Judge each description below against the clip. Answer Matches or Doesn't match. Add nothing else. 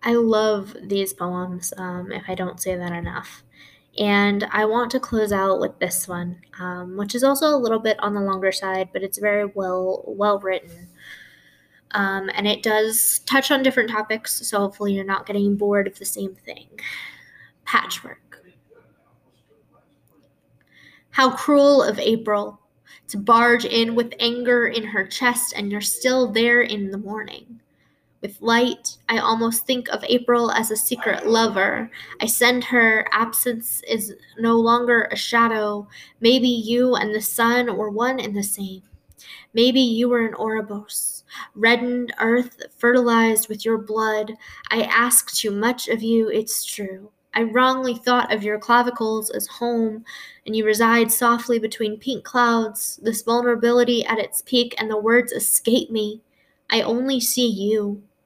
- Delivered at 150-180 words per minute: Matches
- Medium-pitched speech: Doesn't match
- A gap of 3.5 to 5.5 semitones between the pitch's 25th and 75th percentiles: Doesn't match